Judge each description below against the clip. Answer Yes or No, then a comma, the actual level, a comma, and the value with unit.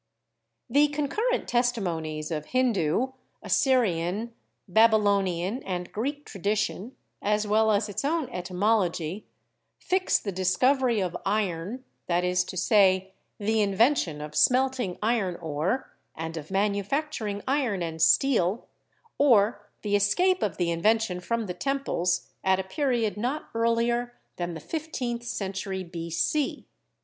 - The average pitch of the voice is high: Yes, high, 205 Hz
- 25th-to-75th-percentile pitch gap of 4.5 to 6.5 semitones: Yes, average, 5.2 semitones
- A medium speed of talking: No, slow, 130 wpm